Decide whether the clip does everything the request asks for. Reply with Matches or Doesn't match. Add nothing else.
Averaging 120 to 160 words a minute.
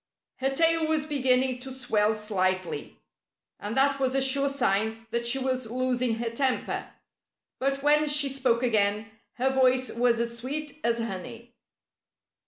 Matches